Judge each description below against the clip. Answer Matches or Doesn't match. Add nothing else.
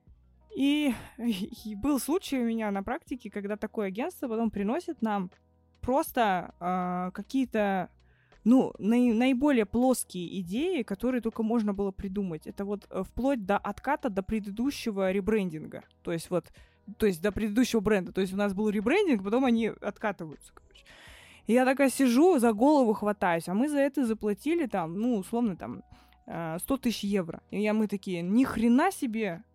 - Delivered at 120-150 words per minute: Doesn't match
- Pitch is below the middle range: Doesn't match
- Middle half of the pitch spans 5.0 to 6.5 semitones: Doesn't match